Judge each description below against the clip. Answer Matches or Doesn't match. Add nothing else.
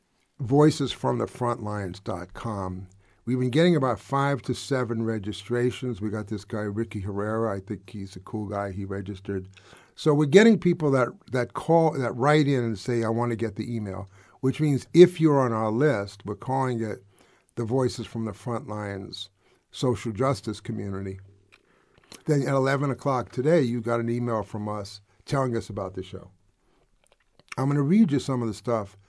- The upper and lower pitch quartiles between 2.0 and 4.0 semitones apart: Doesn't match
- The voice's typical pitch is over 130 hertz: Doesn't match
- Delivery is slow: Doesn't match